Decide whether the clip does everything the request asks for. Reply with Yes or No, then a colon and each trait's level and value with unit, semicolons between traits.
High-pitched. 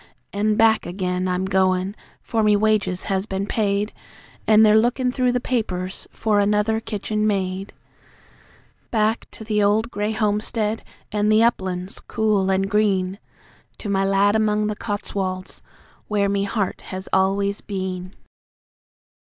Yes: high, 205 Hz